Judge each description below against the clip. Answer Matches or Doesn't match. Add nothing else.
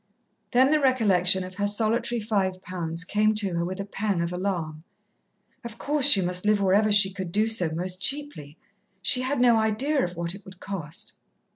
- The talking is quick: Doesn't match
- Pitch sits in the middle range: Doesn't match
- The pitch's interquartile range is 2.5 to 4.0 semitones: Matches